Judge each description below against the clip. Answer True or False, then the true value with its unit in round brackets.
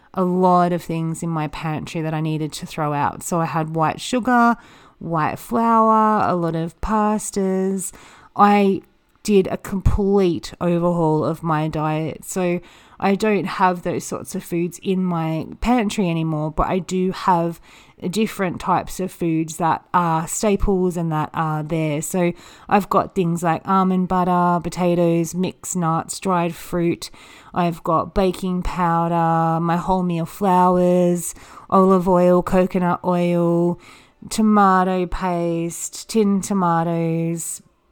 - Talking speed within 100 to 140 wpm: True (135 wpm)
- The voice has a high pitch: False (175 Hz)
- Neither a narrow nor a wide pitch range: False (2.3 semitones)